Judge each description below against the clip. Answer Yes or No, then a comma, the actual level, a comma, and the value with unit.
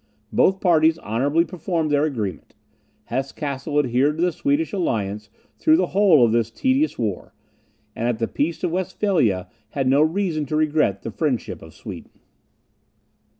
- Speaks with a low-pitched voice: No, medium, 150 Hz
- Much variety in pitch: Yes, wide, 6.7 semitones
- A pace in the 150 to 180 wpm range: Yes, average, 155 wpm